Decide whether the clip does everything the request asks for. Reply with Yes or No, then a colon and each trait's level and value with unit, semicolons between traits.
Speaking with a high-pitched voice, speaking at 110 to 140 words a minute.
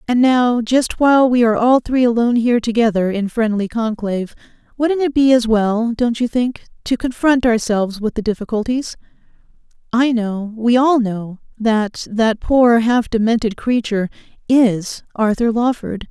No: high, 230 Hz; average, 155 wpm